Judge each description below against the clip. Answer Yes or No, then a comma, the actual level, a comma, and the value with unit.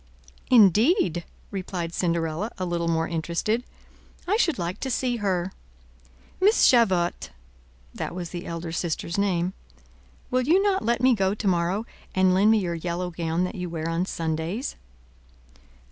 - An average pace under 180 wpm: Yes, average, 145 wpm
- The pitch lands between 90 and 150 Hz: No, medium, 180 Hz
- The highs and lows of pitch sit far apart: No, average, 4.2 semitones